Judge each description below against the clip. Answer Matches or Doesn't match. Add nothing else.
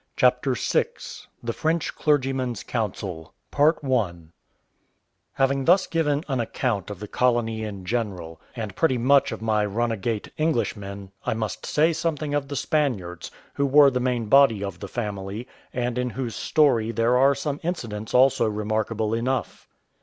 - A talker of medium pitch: Doesn't match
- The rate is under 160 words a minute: Matches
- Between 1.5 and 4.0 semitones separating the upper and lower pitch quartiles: Doesn't match